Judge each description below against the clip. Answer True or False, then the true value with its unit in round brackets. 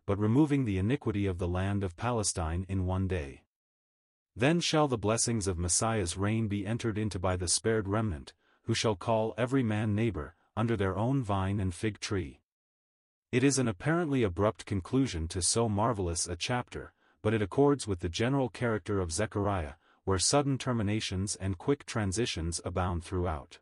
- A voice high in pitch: False (105 Hz)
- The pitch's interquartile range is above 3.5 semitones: True (4.0 semitones)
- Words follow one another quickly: False (170 wpm)